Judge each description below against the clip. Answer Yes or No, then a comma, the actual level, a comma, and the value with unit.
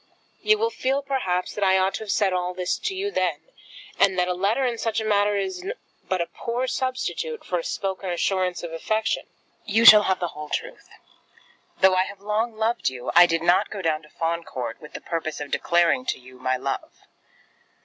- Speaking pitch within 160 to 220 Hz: Yes, high, 190 Hz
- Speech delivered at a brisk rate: Yes, fast, 210 wpm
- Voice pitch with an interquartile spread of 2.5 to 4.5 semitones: No, average, 5.0 semitones